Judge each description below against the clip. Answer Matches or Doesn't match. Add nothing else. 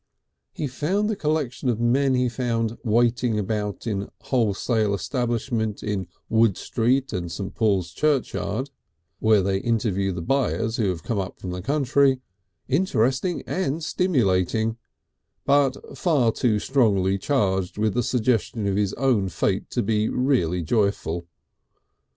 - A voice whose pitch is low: Matches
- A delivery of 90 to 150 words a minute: Matches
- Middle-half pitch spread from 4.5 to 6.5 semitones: Matches